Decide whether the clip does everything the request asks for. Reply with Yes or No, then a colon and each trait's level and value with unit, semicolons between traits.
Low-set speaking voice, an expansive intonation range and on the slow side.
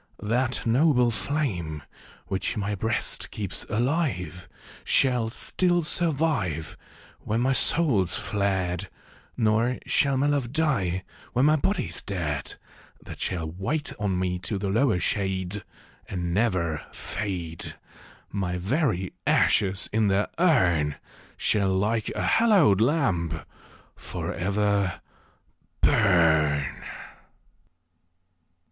Yes: low, 100 Hz; wide, 6.2 semitones; slow, 105 wpm